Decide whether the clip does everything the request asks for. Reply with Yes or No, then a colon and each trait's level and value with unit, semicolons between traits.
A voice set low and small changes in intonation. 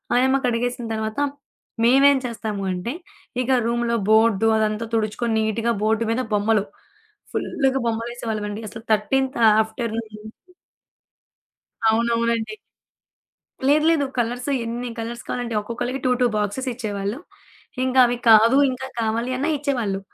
No: high, 230 Hz; narrow, 2.2 semitones